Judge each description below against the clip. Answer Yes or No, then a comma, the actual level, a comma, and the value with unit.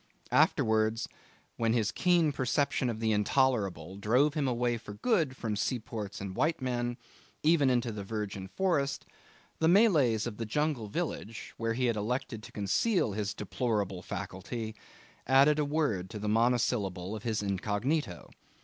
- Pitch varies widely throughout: No, average, 4.7 semitones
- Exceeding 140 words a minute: Yes, average, 150 wpm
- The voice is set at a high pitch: No, low, 115 Hz